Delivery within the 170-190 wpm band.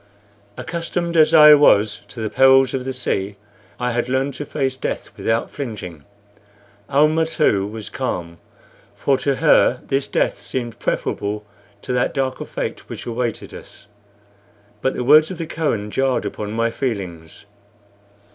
No: average, 150 wpm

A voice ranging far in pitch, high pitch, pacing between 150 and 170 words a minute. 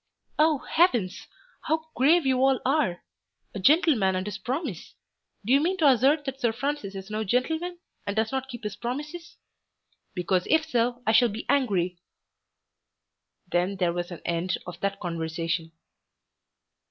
Yes: wide, 7.5 semitones; high, 240 Hz; average, 155 wpm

